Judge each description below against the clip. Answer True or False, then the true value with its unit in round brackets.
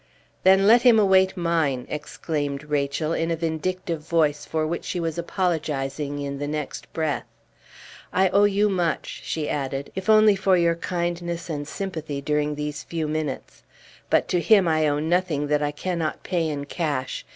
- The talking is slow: False (170 wpm)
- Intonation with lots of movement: False (3.4 semitones)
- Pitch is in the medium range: True (160 Hz)